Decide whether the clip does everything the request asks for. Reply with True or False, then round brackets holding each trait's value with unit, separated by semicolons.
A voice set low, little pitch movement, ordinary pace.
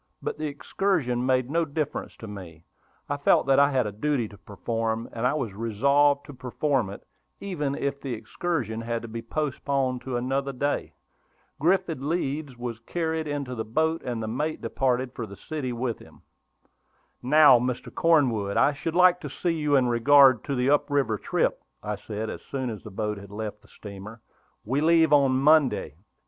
False (130 Hz; 4.3 semitones; 185 wpm)